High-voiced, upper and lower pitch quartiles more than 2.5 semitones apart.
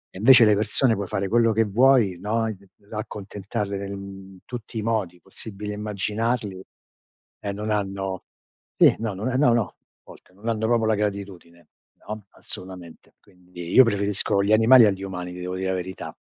No: low, 105 Hz; average, 2.9 semitones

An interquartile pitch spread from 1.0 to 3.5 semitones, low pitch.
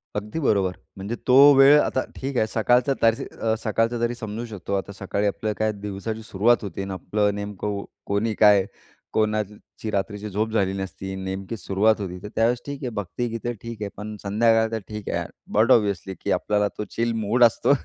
Yes: narrow, 2.4 semitones; low, 105 Hz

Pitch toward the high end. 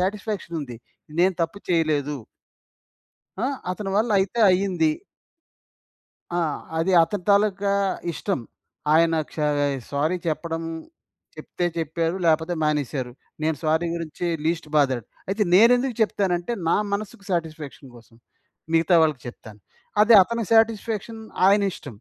No: medium, 170 Hz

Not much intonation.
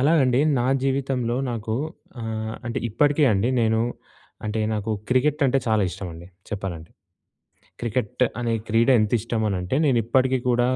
No: average, 3.2 semitones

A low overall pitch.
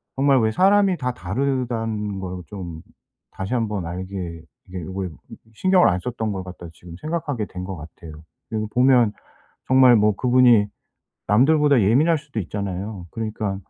Yes: low, 110 Hz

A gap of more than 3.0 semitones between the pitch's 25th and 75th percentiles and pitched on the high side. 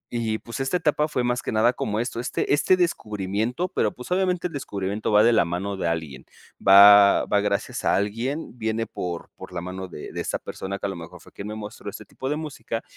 No: average, 4.2 semitones; low, 110 Hz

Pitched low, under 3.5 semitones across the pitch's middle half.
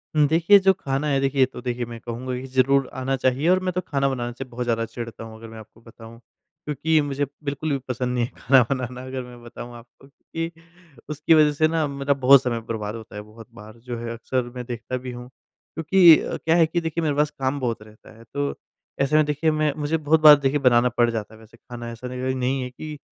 No: low, 130 Hz; average, 3.8 semitones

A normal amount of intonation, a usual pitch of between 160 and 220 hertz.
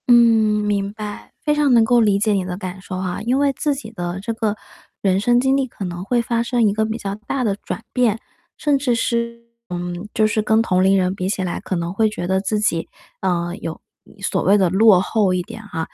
Yes: average, 3.9 semitones; high, 210 Hz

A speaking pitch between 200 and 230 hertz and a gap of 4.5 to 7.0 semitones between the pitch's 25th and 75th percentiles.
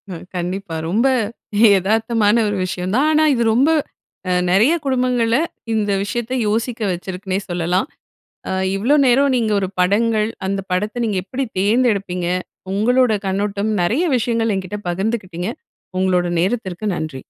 No: high, 210 Hz; average, 4.1 semitones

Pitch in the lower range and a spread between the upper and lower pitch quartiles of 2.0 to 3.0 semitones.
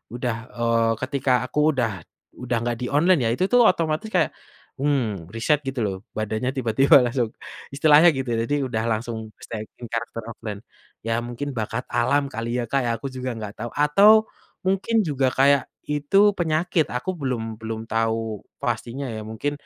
No: low, 125 Hz; average, 4.2 semitones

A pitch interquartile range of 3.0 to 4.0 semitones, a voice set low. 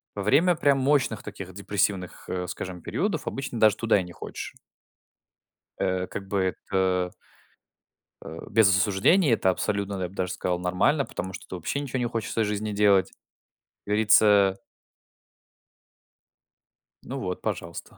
Yes: average, 3.5 semitones; low, 100 Hz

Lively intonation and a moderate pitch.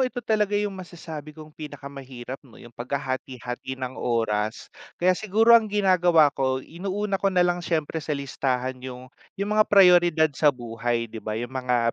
Yes: wide, 6.4 semitones; medium, 145 Hz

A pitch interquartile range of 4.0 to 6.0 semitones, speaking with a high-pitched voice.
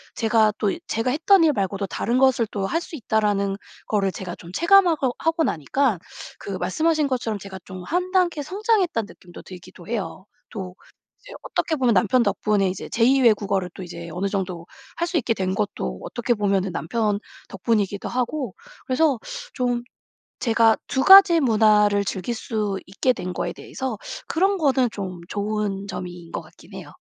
Yes: wide, 5.5 semitones; high, 220 Hz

